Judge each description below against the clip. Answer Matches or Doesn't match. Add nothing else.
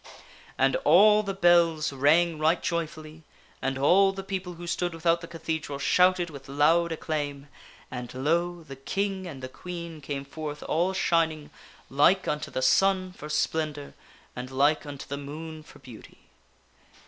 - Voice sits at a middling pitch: Matches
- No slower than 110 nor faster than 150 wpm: Doesn't match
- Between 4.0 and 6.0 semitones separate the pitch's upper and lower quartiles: Doesn't match